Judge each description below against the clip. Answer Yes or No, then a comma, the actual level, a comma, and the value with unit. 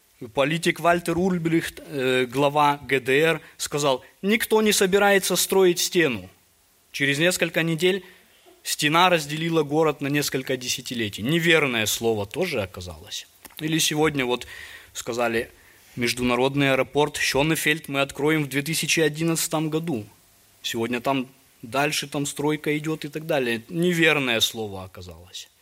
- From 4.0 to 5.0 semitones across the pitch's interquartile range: Yes, average, 4.5 semitones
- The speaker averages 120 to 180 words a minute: No, slow, 110 wpm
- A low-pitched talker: No, medium, 150 Hz